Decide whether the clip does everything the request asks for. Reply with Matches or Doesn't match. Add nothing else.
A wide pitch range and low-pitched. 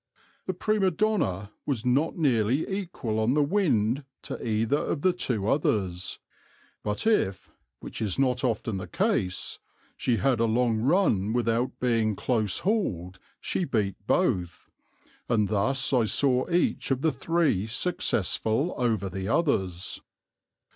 Matches